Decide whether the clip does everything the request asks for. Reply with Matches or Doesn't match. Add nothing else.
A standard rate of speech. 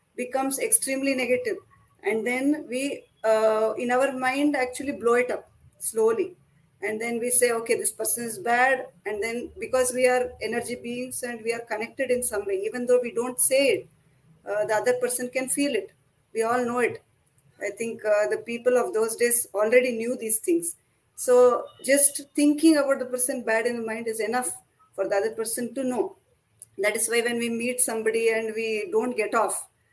Doesn't match